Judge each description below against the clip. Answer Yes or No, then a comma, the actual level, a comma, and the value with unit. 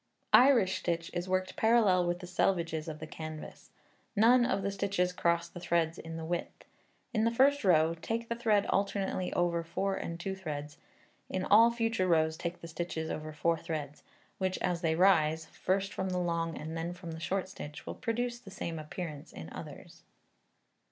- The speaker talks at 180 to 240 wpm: Yes, average, 185 wpm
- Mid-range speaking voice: Yes, medium, 175 Hz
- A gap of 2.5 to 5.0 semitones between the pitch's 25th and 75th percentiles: Yes, average, 3.3 semitones